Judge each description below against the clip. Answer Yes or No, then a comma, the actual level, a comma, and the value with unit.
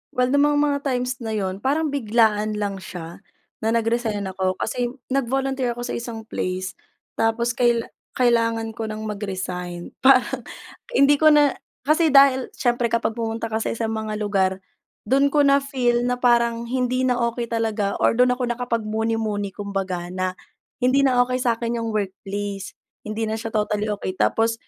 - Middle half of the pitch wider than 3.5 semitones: No, average, 3.2 semitones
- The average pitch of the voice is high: Yes, high, 230 Hz